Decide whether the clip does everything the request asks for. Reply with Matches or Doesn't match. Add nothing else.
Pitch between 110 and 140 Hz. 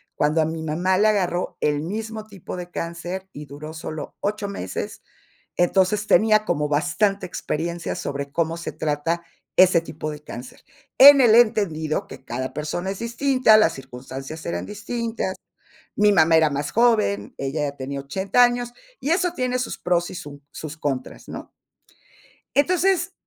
Doesn't match